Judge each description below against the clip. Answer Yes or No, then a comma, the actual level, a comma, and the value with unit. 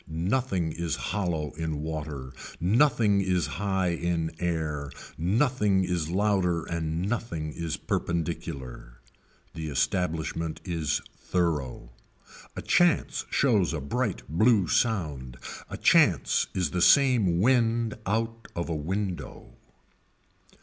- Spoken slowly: Yes, slow, 110 wpm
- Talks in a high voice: No, very low, 85 Hz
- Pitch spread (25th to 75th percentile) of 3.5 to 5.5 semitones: Yes, average, 4.6 semitones